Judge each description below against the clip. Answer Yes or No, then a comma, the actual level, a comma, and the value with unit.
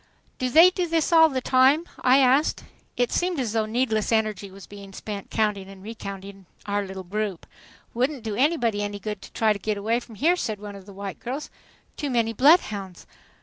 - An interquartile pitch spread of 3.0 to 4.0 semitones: No, average, 4.4 semitones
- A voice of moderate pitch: No, high, 220 Hz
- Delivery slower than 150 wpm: No, average, 200 wpm